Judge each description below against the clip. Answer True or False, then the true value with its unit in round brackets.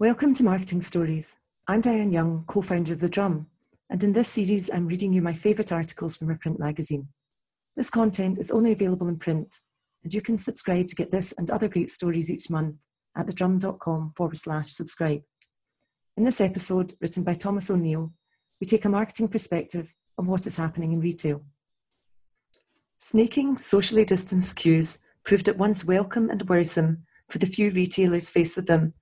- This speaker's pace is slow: False (175 wpm)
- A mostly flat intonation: False (3.7 semitones)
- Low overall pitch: False (180 Hz)